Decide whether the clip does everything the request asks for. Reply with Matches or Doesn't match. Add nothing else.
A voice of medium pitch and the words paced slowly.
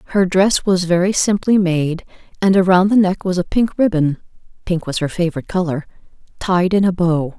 Doesn't match